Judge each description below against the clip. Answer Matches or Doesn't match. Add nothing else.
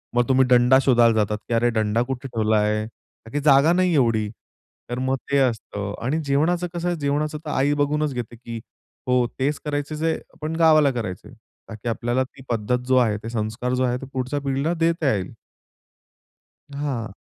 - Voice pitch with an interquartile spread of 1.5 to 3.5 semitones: Doesn't match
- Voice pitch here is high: Doesn't match